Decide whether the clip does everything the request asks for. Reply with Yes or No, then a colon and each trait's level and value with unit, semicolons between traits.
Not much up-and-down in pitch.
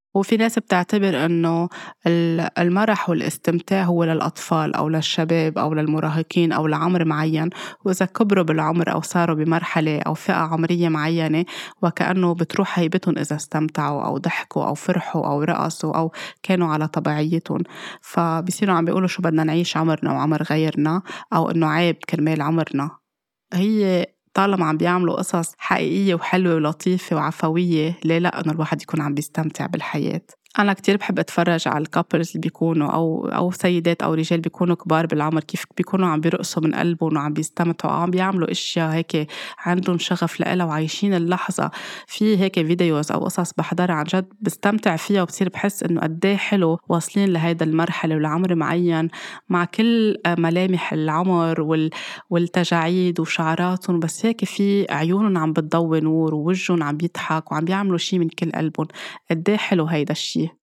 Yes: narrow, 2.3 semitones